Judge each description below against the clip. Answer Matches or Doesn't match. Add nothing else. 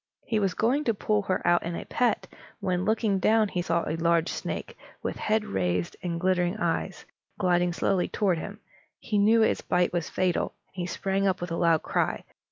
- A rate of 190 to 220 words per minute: Matches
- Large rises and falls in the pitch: Doesn't match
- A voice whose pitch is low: Doesn't match